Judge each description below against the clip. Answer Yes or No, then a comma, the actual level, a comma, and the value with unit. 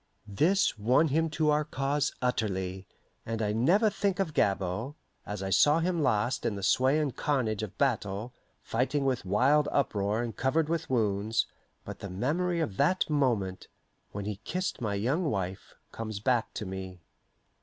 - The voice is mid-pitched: No, low, 120 Hz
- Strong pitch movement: Yes, wide, 6.5 semitones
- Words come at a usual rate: Yes, average, 165 wpm